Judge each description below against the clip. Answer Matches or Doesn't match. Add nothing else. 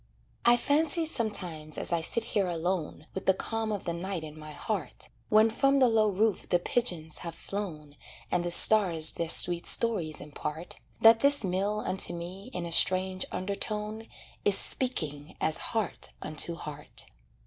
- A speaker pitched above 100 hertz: Matches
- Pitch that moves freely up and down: Doesn't match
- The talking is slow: Doesn't match